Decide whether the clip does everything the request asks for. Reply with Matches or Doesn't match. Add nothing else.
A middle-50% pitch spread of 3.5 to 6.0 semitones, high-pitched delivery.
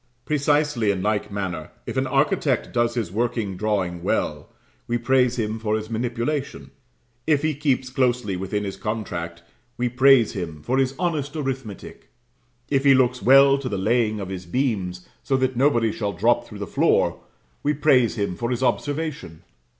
Doesn't match